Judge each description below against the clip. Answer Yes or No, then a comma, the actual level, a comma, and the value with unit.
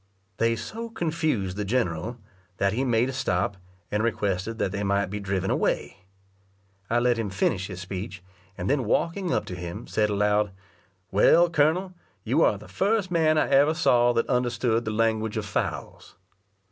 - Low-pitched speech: Yes, low, 115 Hz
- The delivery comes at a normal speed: Yes, average, 170 wpm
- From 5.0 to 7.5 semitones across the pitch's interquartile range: Yes, wide, 5.4 semitones